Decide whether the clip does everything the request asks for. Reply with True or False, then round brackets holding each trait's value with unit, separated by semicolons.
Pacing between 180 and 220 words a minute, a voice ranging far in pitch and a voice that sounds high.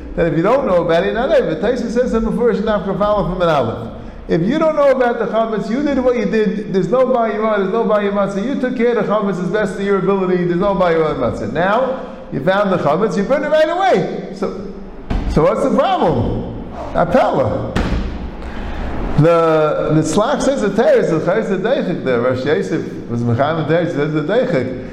True (200 wpm; 6.0 semitones; 200 Hz)